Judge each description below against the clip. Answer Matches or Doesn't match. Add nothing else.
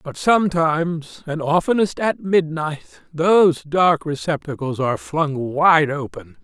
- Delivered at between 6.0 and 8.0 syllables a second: Doesn't match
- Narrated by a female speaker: Doesn't match